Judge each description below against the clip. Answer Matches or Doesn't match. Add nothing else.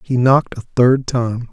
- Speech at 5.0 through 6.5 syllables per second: Doesn't match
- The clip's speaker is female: Doesn't match